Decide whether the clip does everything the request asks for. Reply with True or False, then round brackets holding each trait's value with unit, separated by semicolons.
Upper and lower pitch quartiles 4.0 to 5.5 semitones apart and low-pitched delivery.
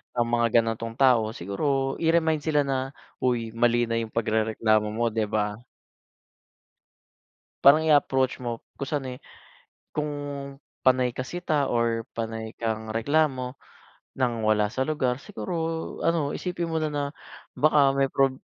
True (4.3 semitones; 130 Hz)